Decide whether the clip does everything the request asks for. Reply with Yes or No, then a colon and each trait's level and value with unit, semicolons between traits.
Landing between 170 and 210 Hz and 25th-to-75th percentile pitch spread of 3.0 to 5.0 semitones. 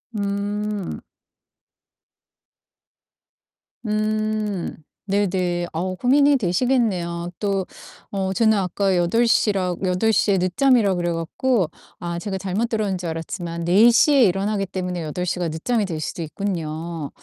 Yes: high, 190 Hz; average, 3.5 semitones